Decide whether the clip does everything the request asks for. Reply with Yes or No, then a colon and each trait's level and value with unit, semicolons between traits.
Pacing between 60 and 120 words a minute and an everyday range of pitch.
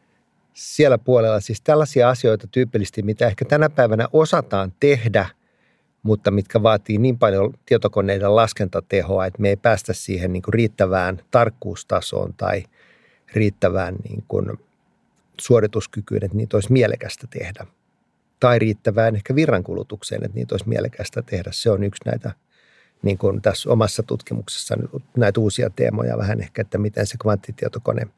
No: average, 135 wpm; average, 3.2 semitones